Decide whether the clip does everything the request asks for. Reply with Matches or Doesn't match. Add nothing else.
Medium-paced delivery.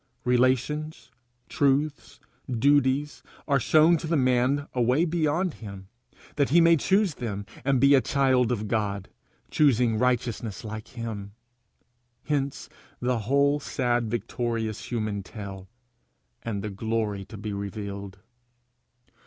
Doesn't match